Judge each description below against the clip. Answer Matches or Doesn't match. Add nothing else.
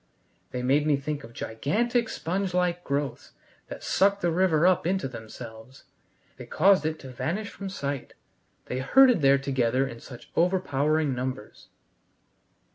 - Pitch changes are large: Matches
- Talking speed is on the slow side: Doesn't match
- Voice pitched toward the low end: Doesn't match